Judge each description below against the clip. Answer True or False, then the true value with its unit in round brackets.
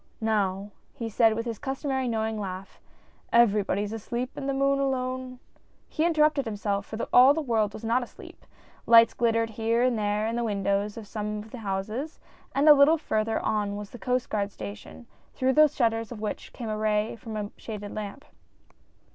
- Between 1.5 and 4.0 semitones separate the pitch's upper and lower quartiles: True (3.4 semitones)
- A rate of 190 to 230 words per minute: True (195 wpm)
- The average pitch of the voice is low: False (225 Hz)